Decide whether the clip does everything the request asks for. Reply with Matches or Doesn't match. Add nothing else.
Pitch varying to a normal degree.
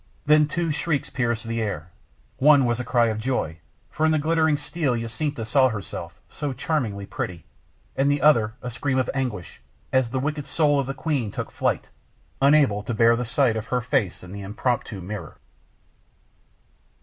Matches